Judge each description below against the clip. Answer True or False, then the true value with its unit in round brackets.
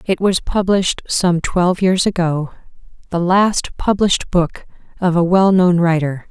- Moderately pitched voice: True (180 Hz)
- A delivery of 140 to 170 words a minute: True (145 wpm)